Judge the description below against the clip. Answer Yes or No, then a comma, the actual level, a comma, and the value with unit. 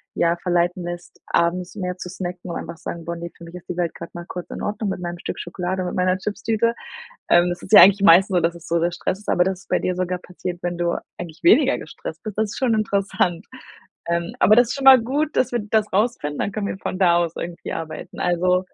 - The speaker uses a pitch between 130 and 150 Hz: No, medium, 180 Hz